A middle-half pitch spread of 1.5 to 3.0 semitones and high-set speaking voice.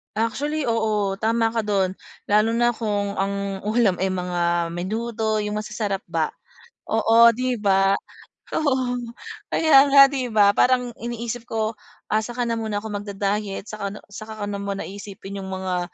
Yes: narrow, 2.6 semitones; high, 215 Hz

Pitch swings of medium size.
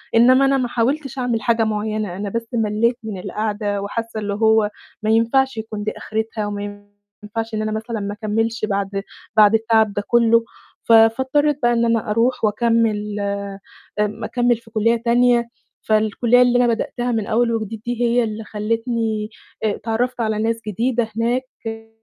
No: narrow, 1.8 semitones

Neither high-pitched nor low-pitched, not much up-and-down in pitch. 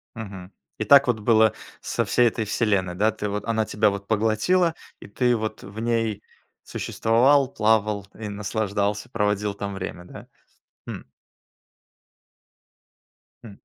No: low, 110 Hz; narrow, 2.0 semitones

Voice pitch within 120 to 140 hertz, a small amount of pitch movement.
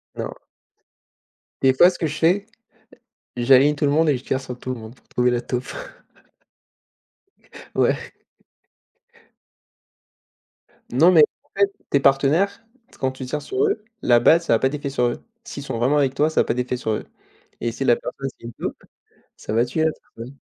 No: low, 135 Hz; average, 4.0 semitones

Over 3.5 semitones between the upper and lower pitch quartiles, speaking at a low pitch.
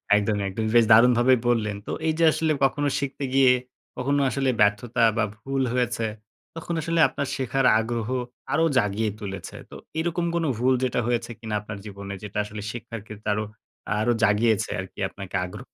Yes: average, 4.0 semitones; low, 115 Hz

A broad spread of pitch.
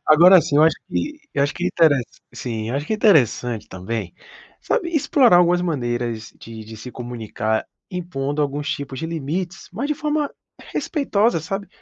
Yes: wide, 7.9 semitones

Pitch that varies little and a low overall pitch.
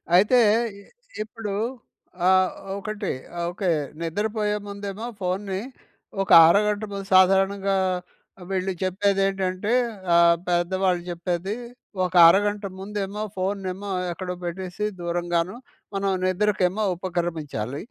No: narrow, 2.3 semitones; high, 190 Hz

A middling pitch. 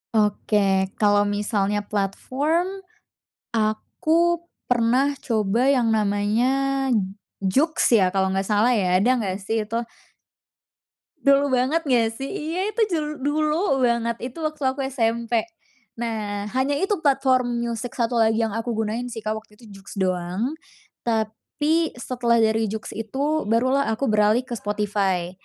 No: high, 230 Hz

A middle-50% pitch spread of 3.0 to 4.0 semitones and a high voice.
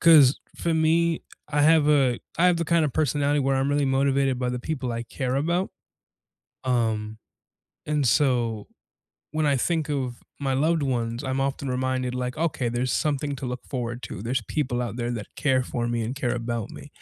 No: average, 3.3 semitones; low, 135 Hz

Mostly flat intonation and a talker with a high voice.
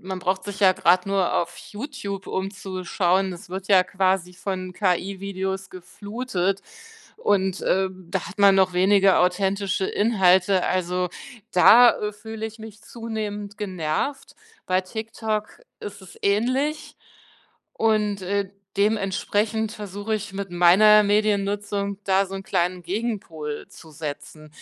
Yes: narrow, 2.2 semitones; high, 195 Hz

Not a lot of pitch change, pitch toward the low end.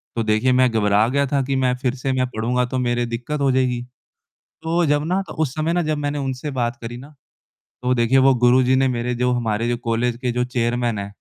Yes: narrow, 2.2 semitones; low, 125 Hz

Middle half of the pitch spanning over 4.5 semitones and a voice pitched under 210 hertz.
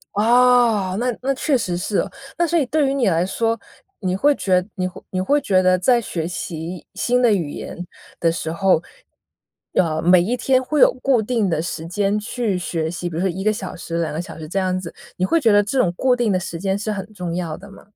Yes: average, 5.3 semitones; high, 195 Hz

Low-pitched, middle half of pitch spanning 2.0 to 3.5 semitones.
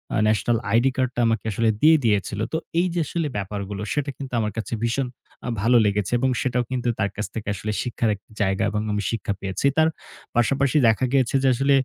No: low, 120 Hz; average, 4.3 semitones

